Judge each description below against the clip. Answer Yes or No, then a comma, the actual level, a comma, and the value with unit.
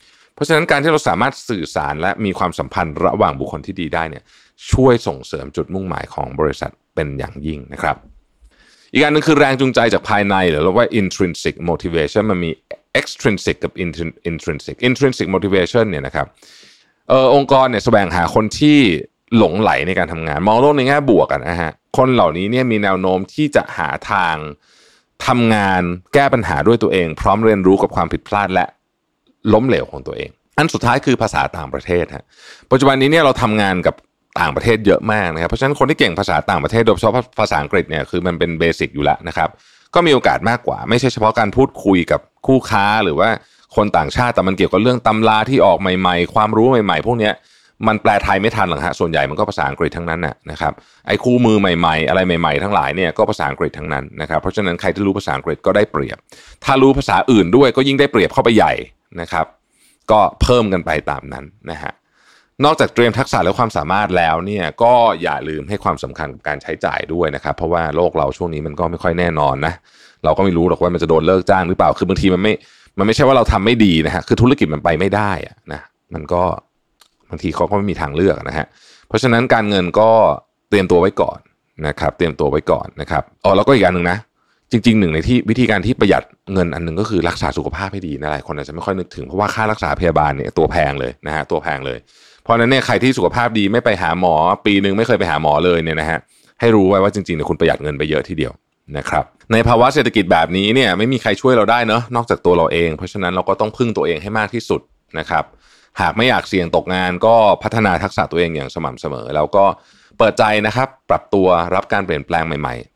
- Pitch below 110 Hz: Yes, low, 100 Hz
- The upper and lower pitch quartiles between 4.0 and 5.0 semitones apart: No, wide, 5.6 semitones